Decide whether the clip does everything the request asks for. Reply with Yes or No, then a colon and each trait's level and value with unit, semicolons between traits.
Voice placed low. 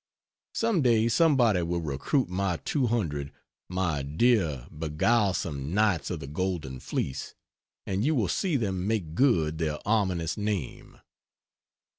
Yes: very low, 95 Hz